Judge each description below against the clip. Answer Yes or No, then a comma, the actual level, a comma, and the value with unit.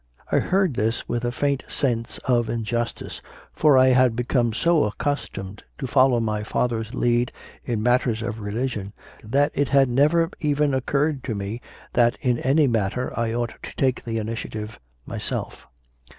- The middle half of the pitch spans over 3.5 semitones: No, average, 3.1 semitones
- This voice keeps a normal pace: Yes, average, 165 wpm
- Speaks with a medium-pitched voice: No, low, 120 Hz